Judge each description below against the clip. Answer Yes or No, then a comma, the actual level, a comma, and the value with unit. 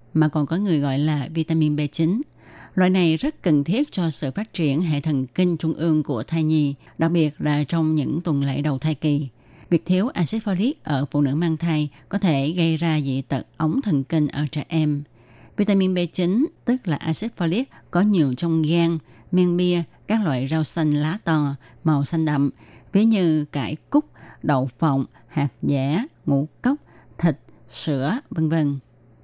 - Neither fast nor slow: Yes, average, 185 wpm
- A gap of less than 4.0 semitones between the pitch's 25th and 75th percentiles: Yes, average, 3.4 semitones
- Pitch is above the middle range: No, medium, 155 Hz